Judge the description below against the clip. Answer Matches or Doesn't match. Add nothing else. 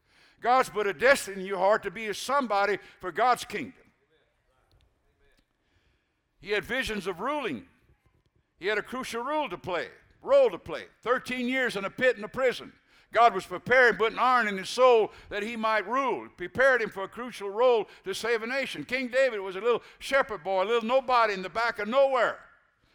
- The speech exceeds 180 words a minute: Matches